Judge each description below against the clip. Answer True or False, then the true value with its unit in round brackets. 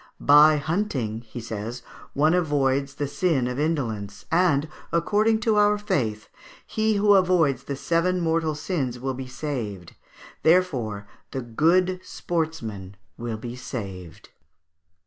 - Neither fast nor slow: False (125 wpm)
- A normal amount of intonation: False (6.8 semitones)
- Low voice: False (145 Hz)